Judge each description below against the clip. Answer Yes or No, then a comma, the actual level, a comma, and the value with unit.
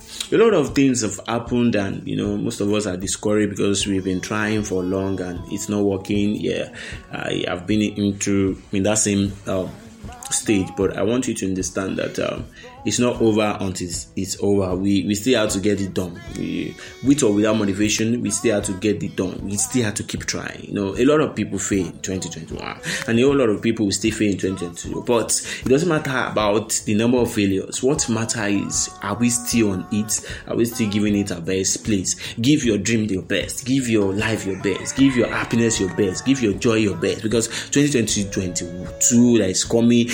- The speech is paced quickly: Yes, fast, 215 wpm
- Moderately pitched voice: No, low, 105 Hz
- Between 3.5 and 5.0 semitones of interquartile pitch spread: No, average, 2.9 semitones